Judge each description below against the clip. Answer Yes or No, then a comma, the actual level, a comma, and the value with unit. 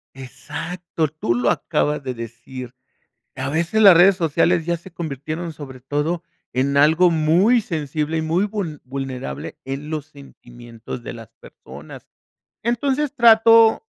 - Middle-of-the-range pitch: Yes, medium, 155 Hz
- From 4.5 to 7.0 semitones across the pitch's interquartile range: Yes, average, 5.0 semitones